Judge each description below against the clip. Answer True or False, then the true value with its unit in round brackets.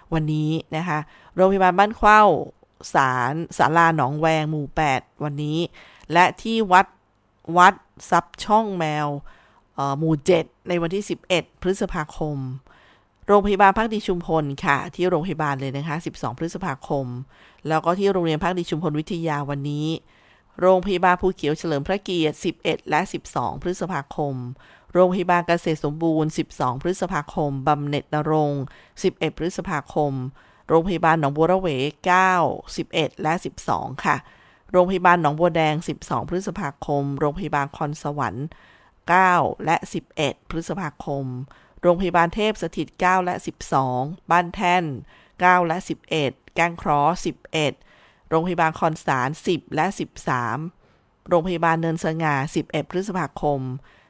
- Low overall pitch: False (160 Hz)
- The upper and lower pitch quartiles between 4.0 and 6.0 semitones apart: False (3.6 semitones)